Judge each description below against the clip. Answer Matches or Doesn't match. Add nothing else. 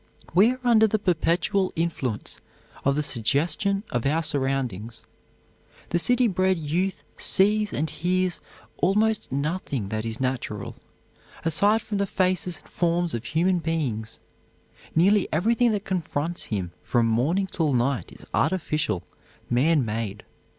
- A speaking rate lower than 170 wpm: Matches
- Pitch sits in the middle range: Matches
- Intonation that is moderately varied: Doesn't match